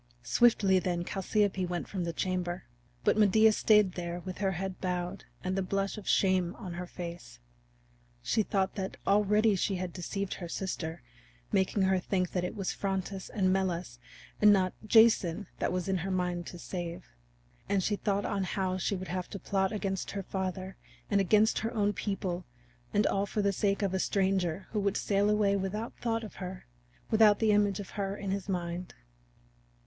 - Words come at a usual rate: Yes, average, 185 wpm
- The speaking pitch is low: No, high, 190 Hz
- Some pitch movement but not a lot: No, narrow, 2.0 semitones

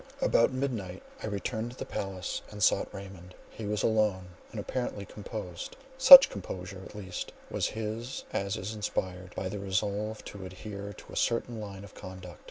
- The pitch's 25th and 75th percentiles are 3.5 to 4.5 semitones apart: No, average, 2.7 semitones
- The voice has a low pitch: Yes, low, 100 Hz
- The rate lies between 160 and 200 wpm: Yes, average, 175 wpm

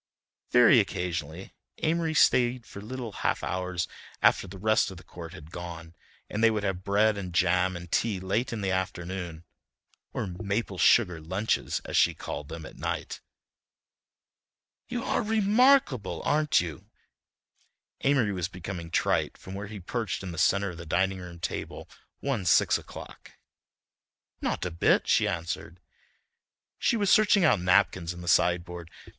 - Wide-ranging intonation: No, average, 4.1 semitones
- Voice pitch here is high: No, very low, 95 Hz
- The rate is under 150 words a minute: No, average, 155 wpm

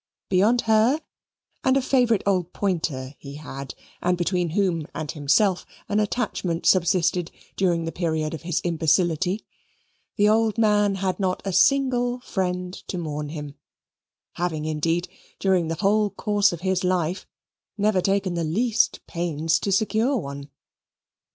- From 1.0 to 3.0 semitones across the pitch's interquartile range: No, average, 4.0 semitones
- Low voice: No, medium, 180 Hz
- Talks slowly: No, average, 145 wpm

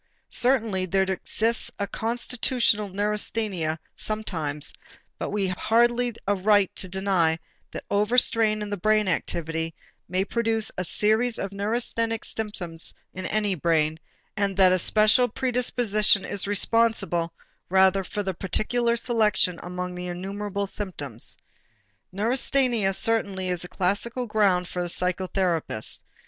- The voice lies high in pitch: Yes, high, 200 Hz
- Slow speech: Yes, slow, 125 wpm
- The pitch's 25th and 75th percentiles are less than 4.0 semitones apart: Yes, average, 3.4 semitones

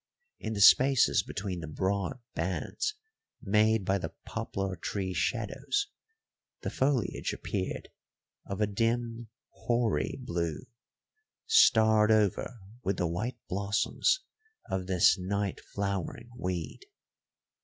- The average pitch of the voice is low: Yes, low, 100 Hz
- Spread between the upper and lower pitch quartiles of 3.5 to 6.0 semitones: Yes, average, 3.9 semitones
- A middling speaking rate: No, slow, 110 wpm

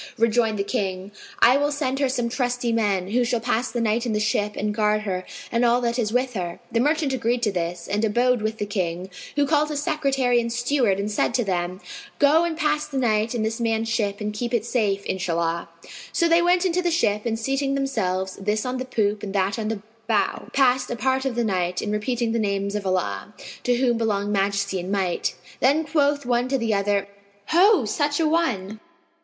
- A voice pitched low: No, high, 230 Hz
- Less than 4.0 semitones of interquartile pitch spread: No, average, 4.3 semitones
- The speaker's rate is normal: No, fast, 220 wpm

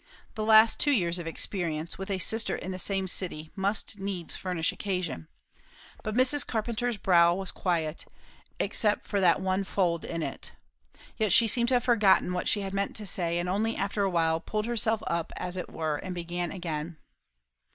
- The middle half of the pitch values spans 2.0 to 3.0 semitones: No, average, 3.7 semitones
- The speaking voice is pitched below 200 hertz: Yes, high, 190 Hz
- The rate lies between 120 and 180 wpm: No, average, 190 wpm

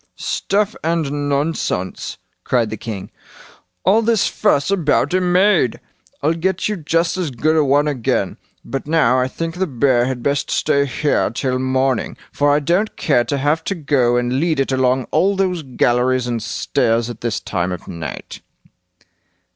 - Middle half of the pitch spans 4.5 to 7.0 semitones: Yes, average, 5.0 semitones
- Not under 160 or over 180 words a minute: Yes, average, 170 wpm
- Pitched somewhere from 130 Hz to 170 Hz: Yes, medium, 140 Hz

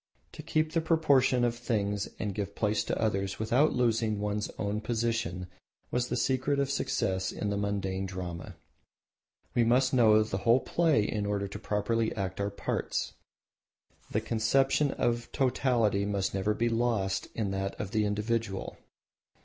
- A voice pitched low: Yes, low, 110 Hz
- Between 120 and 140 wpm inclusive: No, average, 155 wpm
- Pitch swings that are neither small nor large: Yes, average, 3.2 semitones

